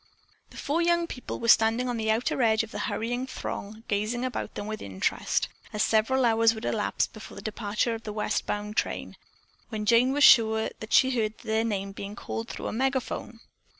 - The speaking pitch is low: No, high, 225 Hz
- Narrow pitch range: Yes, narrow, 2.3 semitones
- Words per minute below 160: No, average, 200 wpm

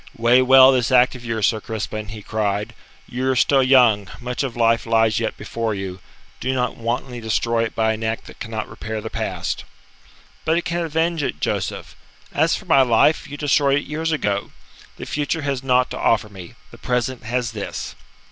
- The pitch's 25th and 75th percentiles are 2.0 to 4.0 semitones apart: Yes, average, 3.3 semitones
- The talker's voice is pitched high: No, low, 120 Hz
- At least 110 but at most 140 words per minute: No, average, 195 wpm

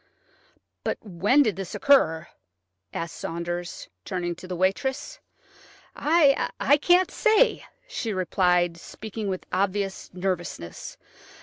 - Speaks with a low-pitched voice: No, high, 190 Hz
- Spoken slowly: Yes, slow, 105 wpm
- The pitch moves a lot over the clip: Yes, wide, 7.3 semitones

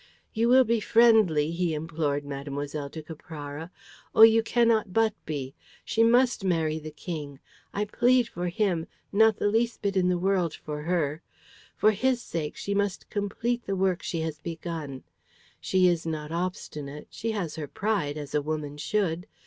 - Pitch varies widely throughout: Yes, wide, 5.9 semitones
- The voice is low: No, medium, 175 Hz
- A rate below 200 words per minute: Yes, average, 170 wpm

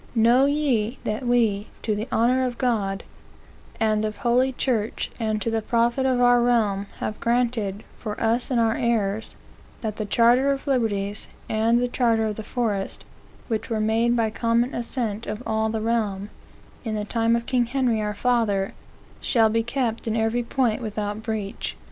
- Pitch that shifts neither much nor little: No, narrow, 2.1 semitones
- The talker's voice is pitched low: No, high, 225 Hz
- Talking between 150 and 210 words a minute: Yes, average, 175 wpm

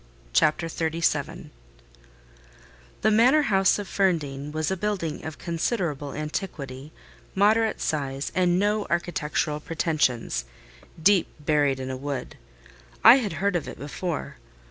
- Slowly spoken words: Yes, slow, 120 wpm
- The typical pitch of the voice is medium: Yes, medium, 165 Hz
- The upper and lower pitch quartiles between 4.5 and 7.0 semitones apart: Yes, average, 4.9 semitones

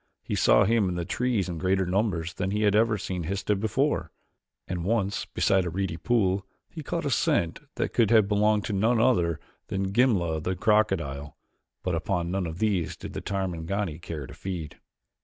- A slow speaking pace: No, average, 190 wpm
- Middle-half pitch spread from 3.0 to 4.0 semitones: Yes, average, 3.6 semitones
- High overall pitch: No, very low, 95 Hz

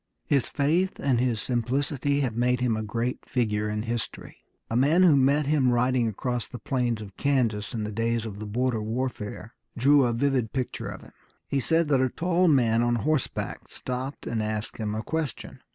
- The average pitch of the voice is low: Yes, low, 125 Hz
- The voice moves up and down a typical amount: Yes, average, 3.6 semitones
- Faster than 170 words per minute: Yes, average, 195 wpm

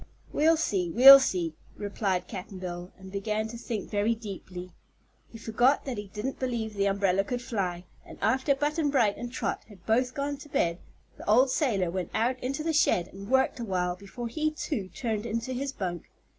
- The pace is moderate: Yes, average, 190 wpm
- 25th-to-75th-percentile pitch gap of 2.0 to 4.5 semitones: No, wide, 5.4 semitones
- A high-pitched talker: Yes, high, 220 Hz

